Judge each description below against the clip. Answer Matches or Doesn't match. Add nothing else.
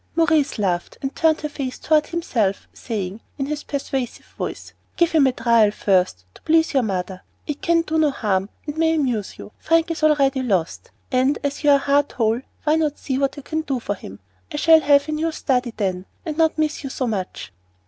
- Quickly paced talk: Matches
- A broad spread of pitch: Matches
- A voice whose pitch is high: Matches